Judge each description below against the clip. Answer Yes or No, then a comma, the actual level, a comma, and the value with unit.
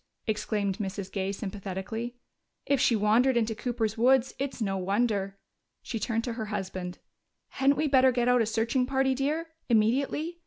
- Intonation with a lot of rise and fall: No, average, 4.2 semitones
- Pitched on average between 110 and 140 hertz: No, high, 230 Hz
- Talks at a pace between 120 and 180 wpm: Yes, average, 160 wpm